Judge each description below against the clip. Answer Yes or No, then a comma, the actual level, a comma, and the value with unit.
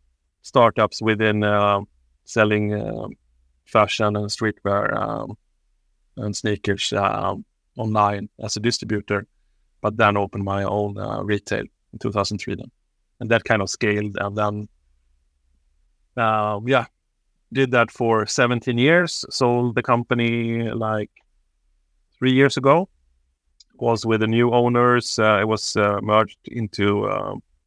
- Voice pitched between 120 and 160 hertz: No, low, 105 Hz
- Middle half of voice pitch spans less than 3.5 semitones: Yes, average, 2.8 semitones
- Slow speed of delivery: Yes, slow, 130 wpm